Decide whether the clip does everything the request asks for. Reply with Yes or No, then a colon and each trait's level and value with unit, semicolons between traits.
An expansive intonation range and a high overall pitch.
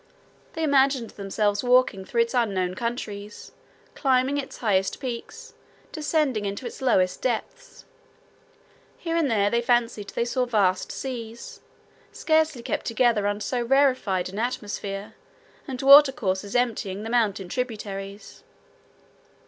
No: average, 4.1 semitones; high, 235 Hz